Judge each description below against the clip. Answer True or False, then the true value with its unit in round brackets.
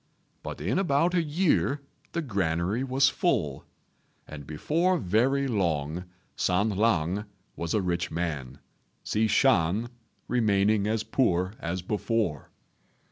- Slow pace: True (120 wpm)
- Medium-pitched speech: False (105 Hz)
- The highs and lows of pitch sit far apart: True (7.5 semitones)